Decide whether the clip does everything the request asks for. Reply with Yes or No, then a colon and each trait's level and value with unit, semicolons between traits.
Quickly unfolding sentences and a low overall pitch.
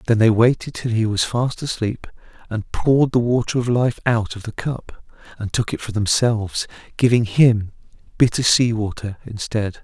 No: average, 175 wpm; low, 115 Hz